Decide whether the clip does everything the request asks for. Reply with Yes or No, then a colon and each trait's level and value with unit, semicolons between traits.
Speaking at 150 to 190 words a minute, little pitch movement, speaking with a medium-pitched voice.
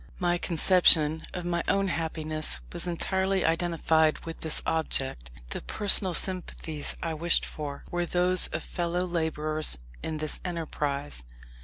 No: slow, 135 wpm; narrow, 2.3 semitones; medium, 165 Hz